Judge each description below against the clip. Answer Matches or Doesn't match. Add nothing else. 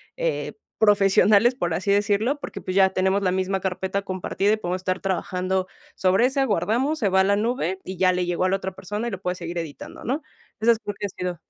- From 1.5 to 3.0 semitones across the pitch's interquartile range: Matches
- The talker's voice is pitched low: Doesn't match